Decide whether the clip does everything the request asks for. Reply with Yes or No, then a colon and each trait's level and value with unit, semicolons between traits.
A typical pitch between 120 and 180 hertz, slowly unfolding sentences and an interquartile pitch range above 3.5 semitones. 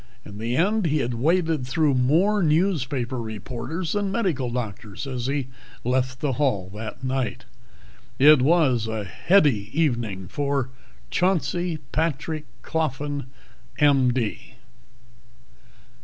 Yes: low, 135 Hz; slow, 110 wpm; average, 4.9 semitones